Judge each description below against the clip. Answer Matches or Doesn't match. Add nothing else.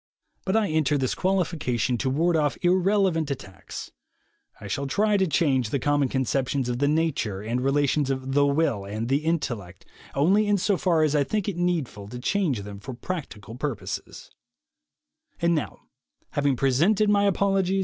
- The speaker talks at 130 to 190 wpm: Matches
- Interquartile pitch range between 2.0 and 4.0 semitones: Doesn't match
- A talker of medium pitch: Matches